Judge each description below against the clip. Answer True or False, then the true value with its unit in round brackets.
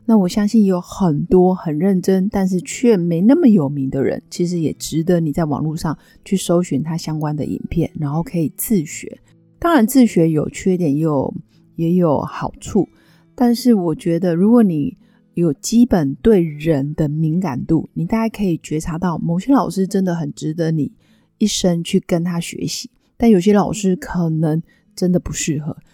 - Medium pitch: True (175 Hz)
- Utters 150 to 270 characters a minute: True (260 characters per minute)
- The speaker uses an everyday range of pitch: True (4.0 semitones)